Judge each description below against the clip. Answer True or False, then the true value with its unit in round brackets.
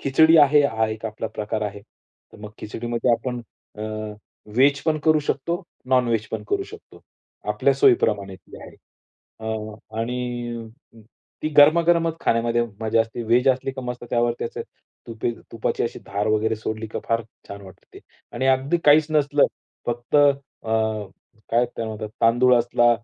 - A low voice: True (120 Hz)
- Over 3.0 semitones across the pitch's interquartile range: True (3.9 semitones)